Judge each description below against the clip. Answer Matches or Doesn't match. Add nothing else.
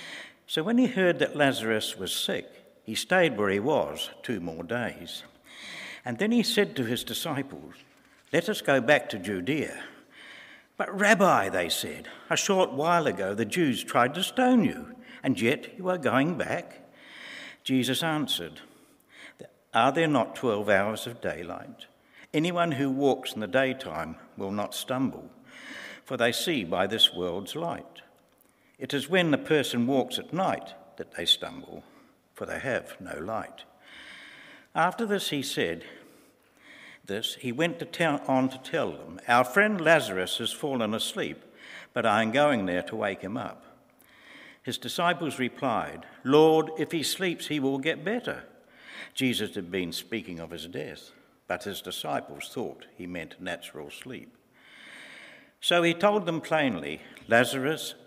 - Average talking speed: Matches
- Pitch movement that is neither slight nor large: Doesn't match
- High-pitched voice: Doesn't match